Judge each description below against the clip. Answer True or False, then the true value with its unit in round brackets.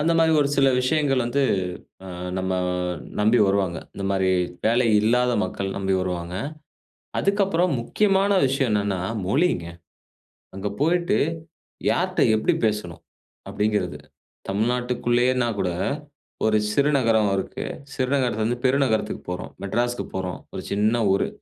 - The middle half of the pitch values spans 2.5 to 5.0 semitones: False (5.5 semitones)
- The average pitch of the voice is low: True (120 Hz)